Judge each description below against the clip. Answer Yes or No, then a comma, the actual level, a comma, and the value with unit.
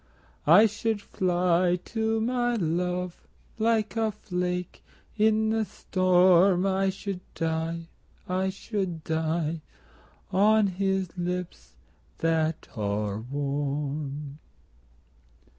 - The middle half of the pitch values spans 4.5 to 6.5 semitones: No, average, 3.9 semitones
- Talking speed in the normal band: No, slow, 90 wpm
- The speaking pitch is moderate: Yes, medium, 180 Hz